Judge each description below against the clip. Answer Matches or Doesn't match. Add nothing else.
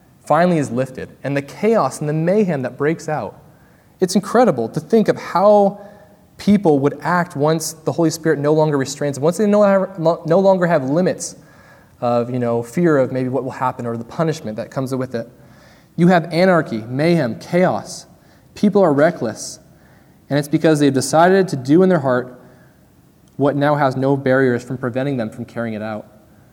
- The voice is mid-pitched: Matches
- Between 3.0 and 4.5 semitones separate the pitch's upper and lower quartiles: Doesn't match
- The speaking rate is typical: Matches